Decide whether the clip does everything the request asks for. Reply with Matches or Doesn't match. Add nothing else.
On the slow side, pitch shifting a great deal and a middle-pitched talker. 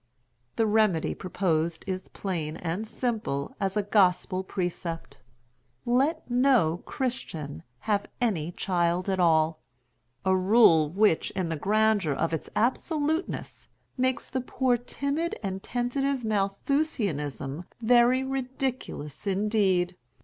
Doesn't match